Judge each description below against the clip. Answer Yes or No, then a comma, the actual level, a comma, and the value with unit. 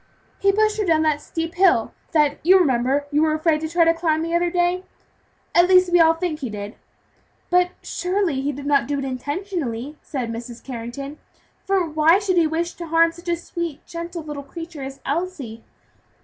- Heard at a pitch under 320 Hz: No, very high, 325 Hz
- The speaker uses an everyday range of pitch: Yes, average, 3.8 semitones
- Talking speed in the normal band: Yes, average, 195 wpm